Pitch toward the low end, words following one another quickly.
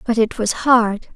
No: high, 225 Hz; fast, 210 wpm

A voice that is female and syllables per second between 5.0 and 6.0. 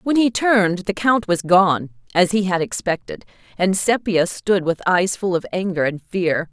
No: female; 4.5 syllables/s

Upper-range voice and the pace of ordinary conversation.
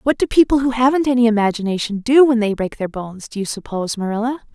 No: high, 230 Hz; fast, 225 wpm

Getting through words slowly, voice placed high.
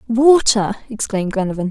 Yes: slow, 105 wpm; high, 220 Hz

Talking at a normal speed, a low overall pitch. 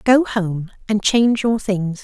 No: average, 175 wpm; high, 210 Hz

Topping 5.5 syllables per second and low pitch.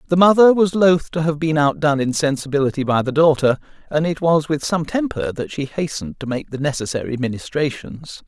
No: 5.7 syllables/s; medium, 150 Hz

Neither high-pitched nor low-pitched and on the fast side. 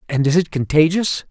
No: medium, 155 Hz; average, 185 wpm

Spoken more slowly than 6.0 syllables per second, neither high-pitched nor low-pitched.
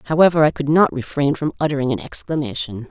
No: 6.4 syllables/s; medium, 145 Hz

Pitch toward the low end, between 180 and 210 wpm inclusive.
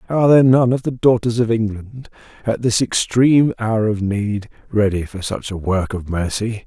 Yes: low, 110 Hz; average, 190 wpm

